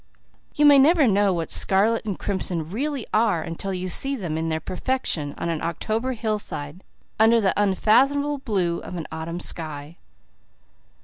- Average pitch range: No, wide, 5.8 semitones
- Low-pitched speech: No, high, 195 Hz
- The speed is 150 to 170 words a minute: Yes, average, 160 wpm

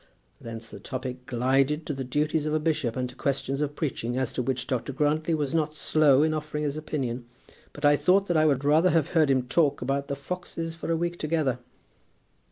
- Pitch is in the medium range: Yes, medium, 145 Hz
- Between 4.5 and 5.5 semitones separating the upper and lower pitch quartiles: No, average, 3.0 semitones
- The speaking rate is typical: No, fast, 215 wpm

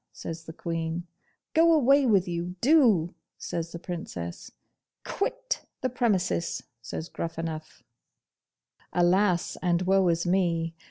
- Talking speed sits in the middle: No, slow, 115 wpm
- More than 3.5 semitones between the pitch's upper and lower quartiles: Yes, average, 4.4 semitones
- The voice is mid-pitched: Yes, medium, 175 Hz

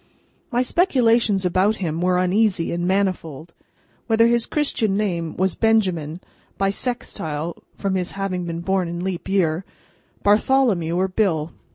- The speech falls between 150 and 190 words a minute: No, slow, 135 wpm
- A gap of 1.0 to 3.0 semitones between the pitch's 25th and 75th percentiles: No, average, 4.1 semitones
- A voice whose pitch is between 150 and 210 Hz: Yes, high, 190 Hz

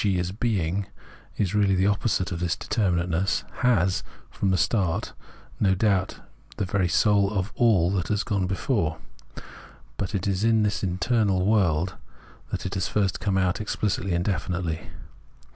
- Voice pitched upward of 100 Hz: No, very low, 95 Hz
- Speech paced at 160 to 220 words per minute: Yes, average, 165 wpm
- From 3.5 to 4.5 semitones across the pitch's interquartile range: No, narrow, 2.5 semitones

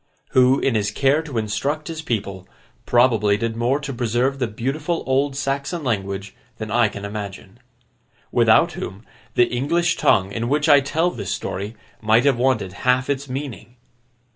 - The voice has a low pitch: Yes, low, 125 Hz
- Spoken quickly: No, average, 165 wpm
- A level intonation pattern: No, average, 4.5 semitones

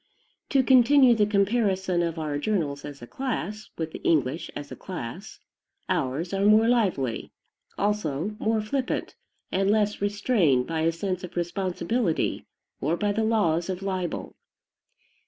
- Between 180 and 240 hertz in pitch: Yes, high, 190 Hz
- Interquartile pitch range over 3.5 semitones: Yes, average, 4.8 semitones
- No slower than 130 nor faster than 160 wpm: Yes, average, 145 wpm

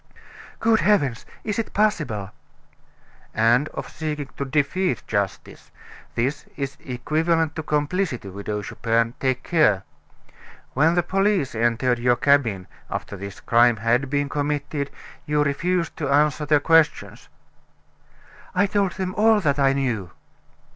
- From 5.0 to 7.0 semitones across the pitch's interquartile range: Yes, average, 5.3 semitones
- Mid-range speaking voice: Yes, medium, 145 Hz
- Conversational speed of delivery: No, slow, 130 wpm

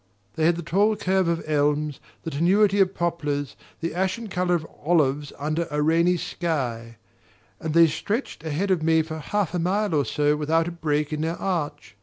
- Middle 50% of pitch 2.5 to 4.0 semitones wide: Yes, average, 3.3 semitones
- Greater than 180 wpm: Yes, average, 190 wpm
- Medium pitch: Yes, medium, 165 Hz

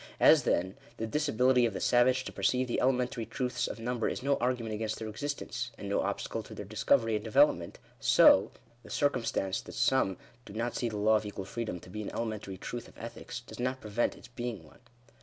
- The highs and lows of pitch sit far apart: No, average, 2.8 semitones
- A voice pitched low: Yes, low, 115 Hz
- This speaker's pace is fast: Yes, fast, 215 wpm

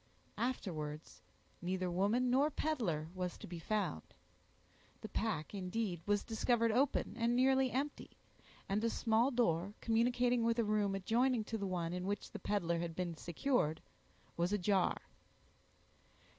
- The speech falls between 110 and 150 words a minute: Yes, average, 145 wpm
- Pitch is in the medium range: No, high, 210 Hz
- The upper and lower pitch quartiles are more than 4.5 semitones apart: Yes, average, 5.2 semitones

